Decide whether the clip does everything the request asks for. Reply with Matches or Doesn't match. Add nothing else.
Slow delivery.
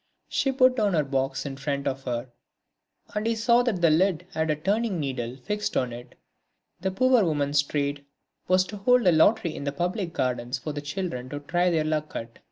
Doesn't match